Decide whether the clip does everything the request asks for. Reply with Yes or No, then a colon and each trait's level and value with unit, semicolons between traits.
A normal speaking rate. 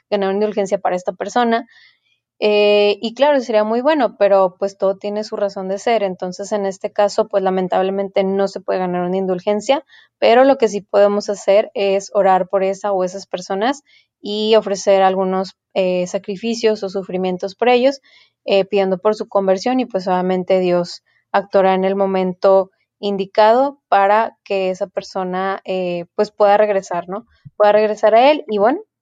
Yes: average, 170 wpm